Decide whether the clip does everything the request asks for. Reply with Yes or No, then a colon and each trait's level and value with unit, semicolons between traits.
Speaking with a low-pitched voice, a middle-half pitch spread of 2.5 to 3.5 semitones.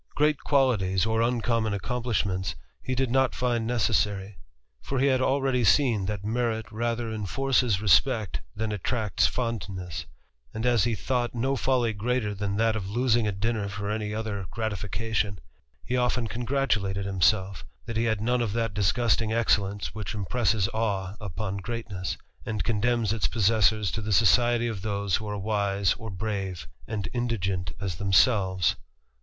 Yes: low, 110 Hz; average, 3.2 semitones